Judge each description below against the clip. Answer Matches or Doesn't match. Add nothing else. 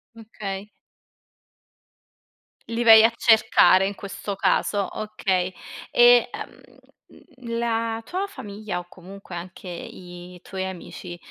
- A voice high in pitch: Matches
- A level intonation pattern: Doesn't match